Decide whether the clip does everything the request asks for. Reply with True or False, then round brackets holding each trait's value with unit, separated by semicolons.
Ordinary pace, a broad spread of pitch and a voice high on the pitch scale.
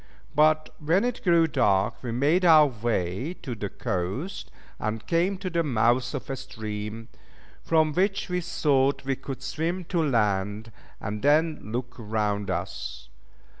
False (150 wpm; 7.1 semitones; 135 Hz)